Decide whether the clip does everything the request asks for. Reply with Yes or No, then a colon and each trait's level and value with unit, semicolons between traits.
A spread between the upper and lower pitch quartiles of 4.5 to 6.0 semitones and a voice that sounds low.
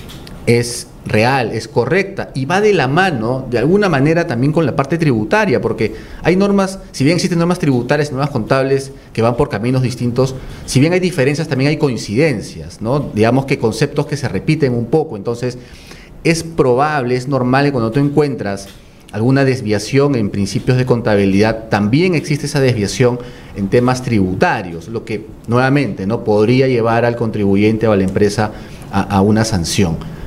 Yes: average, 4.8 semitones; low, 125 Hz